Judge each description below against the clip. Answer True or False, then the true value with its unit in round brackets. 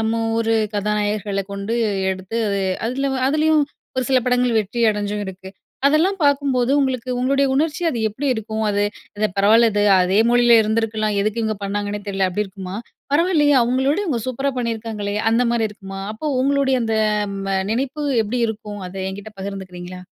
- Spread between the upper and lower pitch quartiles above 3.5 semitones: True (4.2 semitones)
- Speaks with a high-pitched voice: True (225 Hz)